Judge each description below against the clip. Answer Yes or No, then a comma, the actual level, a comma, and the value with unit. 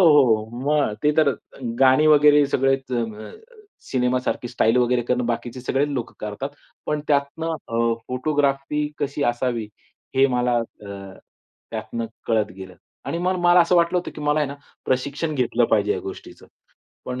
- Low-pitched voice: Yes, low, 130 Hz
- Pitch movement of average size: Yes, average, 4.0 semitones